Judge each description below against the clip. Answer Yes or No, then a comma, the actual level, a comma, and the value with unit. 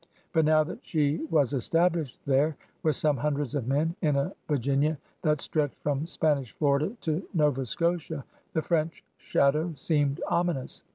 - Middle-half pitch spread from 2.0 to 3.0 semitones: Yes, narrow, 2.4 semitones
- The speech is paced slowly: No, average, 175 wpm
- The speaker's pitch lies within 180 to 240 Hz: No, medium, 150 Hz